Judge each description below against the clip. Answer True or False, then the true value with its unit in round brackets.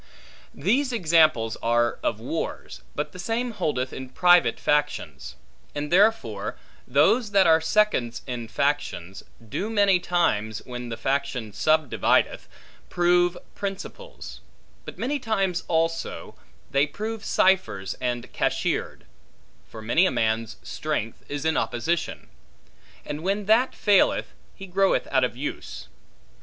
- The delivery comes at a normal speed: False (125 wpm)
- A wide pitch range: True (8.2 semitones)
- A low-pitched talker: False (155 Hz)